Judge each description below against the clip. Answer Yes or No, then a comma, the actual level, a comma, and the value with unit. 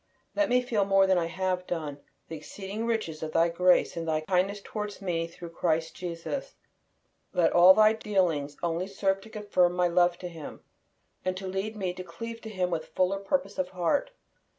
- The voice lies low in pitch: No, medium, 185 Hz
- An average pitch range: Yes, average, 3.0 semitones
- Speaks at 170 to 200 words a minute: Yes, average, 195 wpm